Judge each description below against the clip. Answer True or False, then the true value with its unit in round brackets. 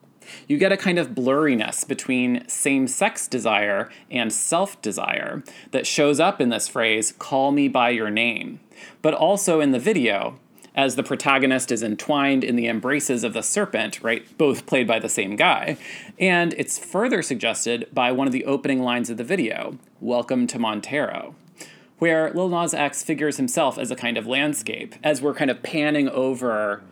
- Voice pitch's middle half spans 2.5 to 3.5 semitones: False (4.0 semitones)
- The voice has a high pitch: False (140 Hz)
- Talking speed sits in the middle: True (180 wpm)